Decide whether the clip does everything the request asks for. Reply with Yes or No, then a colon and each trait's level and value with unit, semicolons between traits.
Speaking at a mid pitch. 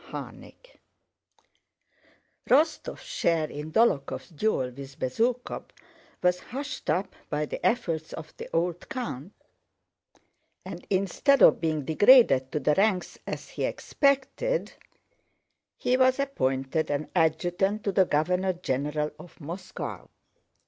Yes: medium, 175 Hz